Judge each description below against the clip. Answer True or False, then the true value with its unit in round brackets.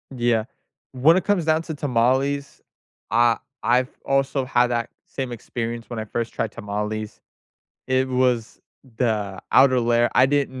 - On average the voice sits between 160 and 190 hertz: False (125 Hz)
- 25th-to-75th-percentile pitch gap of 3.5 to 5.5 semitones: False (2.5 semitones)